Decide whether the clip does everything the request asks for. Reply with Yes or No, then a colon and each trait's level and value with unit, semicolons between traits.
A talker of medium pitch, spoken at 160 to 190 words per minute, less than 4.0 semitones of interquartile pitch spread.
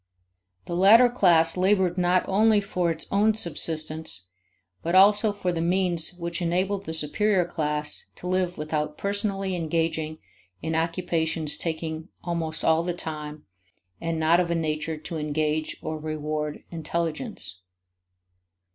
No: medium, 165 Hz; slow, 135 wpm; average, 2.7 semitones